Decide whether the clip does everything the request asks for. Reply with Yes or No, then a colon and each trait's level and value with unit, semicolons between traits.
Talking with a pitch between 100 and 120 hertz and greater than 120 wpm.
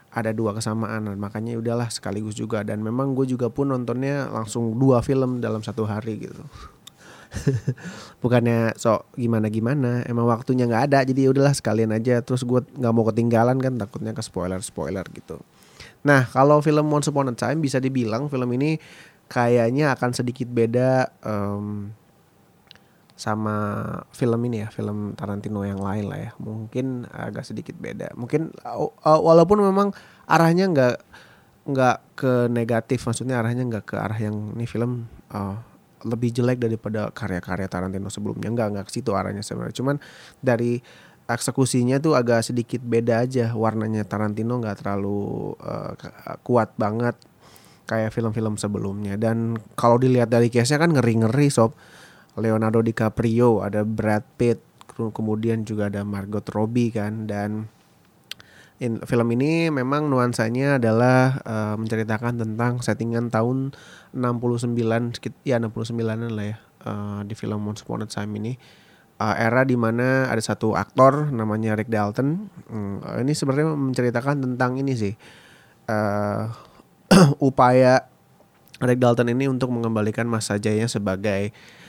Yes: low, 115 Hz; fast, 140 wpm